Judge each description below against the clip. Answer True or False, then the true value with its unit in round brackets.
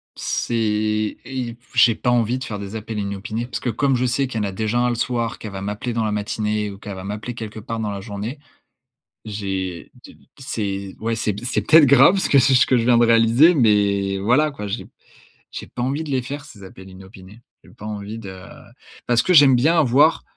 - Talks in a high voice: False (115 Hz)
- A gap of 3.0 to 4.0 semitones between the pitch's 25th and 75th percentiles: True (3.4 semitones)